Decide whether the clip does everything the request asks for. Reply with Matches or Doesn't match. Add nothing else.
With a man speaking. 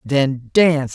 Doesn't match